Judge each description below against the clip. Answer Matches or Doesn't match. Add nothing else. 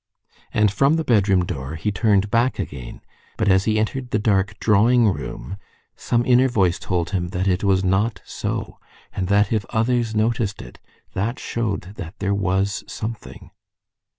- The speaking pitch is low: Matches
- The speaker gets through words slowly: Doesn't match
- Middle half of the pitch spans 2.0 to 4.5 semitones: Matches